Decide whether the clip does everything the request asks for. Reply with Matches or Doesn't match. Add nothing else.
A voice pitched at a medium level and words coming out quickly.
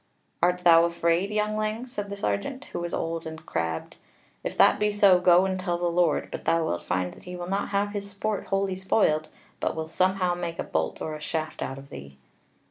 Matches